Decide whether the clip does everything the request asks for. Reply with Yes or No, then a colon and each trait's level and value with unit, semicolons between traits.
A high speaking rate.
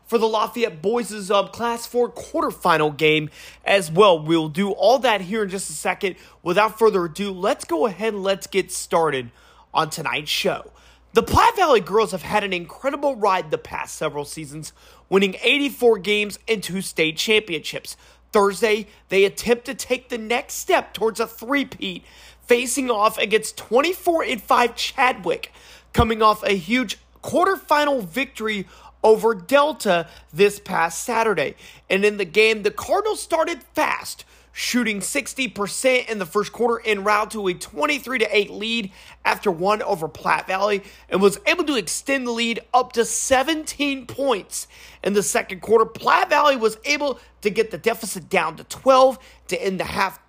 No: average, 160 wpm